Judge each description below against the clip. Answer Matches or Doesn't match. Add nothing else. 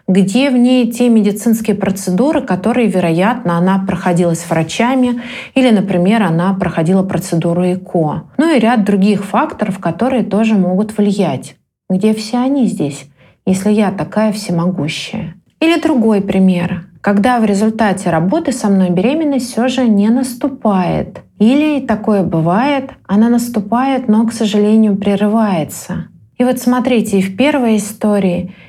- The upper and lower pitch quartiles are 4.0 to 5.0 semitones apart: Matches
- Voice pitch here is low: Doesn't match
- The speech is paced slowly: Doesn't match